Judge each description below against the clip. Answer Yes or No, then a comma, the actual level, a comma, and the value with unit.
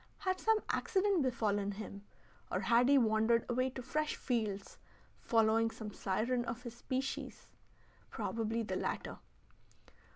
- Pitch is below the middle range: No, high, 235 Hz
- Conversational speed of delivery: No, slow, 130 wpm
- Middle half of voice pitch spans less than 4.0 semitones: Yes, average, 3.1 semitones